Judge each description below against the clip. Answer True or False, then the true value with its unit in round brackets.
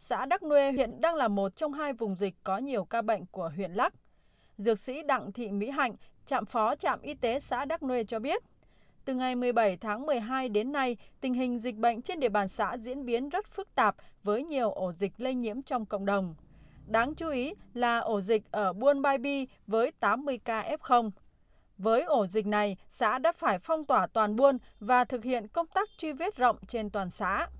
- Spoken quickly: False (215 wpm)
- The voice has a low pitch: False (245 Hz)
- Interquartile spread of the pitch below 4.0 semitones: False (4.7 semitones)